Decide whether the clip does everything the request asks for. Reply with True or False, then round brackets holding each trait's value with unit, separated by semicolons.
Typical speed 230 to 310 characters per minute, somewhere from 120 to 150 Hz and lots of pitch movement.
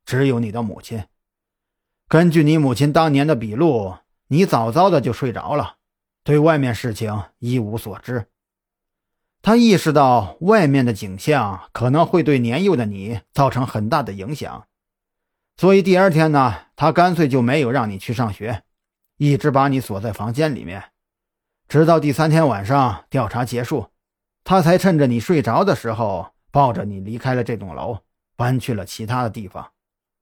True (240 characters per minute; 125 Hz; 6.1 semitones)